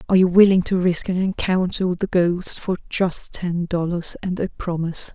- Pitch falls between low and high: Yes, medium, 180 Hz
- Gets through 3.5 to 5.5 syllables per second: Yes, 5.1 syllables/s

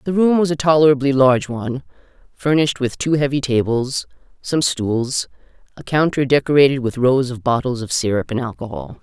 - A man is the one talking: No, female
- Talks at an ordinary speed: Yes, average, 165 wpm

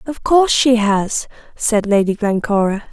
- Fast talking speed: No, average, 145 wpm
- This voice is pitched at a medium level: No, high, 220 Hz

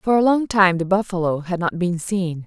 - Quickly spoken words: Yes, fast, 245 wpm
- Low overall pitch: No, medium, 185 Hz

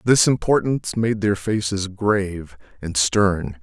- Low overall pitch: Yes, low, 100 Hz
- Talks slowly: Yes, slow, 130 wpm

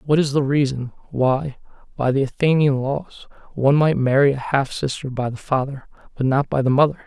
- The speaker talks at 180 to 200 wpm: Yes, average, 195 wpm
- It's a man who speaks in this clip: Yes, male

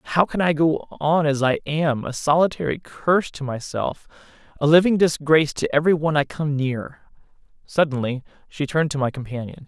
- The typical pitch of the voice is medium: Yes, medium, 150 Hz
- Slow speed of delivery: No, average, 165 wpm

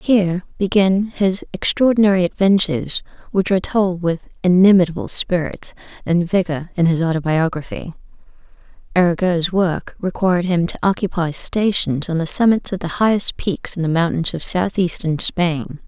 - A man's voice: No, female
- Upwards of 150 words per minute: No, slow, 135 wpm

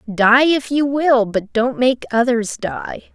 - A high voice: Yes, high, 245 Hz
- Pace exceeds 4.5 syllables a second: No, 3.5 syllables/s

